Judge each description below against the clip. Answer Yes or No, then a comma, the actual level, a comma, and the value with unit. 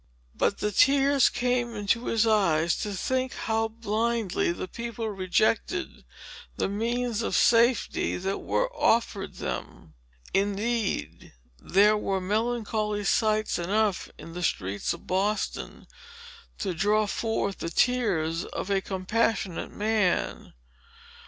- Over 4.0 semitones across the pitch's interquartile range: No, average, 3.2 semitones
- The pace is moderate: No, slow, 120 wpm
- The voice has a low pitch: No, high, 215 Hz